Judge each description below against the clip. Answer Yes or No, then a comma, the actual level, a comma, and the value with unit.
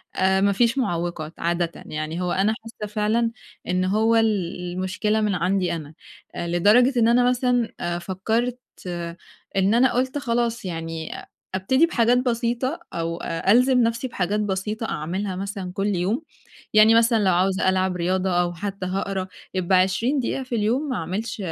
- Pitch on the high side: Yes, high, 200 Hz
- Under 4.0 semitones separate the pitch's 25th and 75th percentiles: No, average, 4.3 semitones